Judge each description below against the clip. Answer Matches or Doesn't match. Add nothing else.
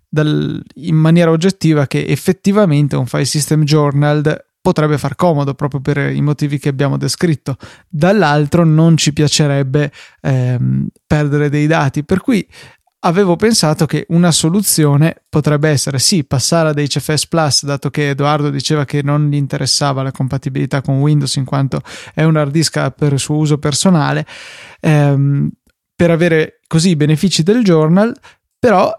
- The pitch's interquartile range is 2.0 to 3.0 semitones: Matches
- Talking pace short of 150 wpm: Doesn't match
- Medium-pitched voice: Matches